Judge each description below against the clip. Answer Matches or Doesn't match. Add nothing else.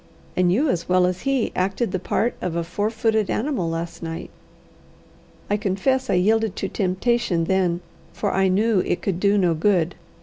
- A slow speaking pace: Doesn't match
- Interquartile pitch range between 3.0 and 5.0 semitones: Matches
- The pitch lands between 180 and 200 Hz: Matches